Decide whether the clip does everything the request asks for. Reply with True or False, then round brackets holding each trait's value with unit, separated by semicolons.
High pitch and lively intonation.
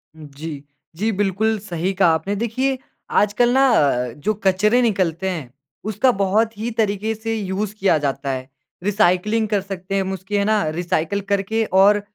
False (200 Hz; 3.5 semitones)